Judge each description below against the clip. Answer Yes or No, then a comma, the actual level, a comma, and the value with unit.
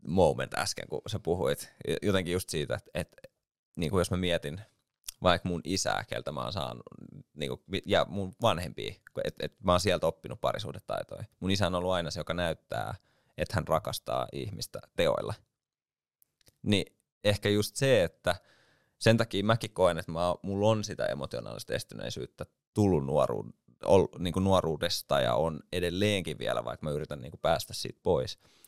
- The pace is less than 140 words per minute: No, fast, 155 wpm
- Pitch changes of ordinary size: Yes, average, 3.0 semitones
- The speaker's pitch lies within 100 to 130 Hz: No, very low, 90 Hz